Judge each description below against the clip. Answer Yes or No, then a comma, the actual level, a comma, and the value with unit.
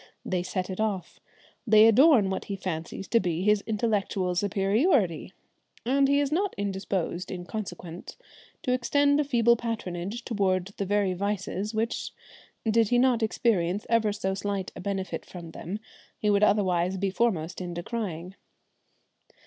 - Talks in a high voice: Yes, high, 200 Hz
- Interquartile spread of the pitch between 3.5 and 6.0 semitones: Yes, average, 3.8 semitones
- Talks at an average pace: Yes, average, 150 wpm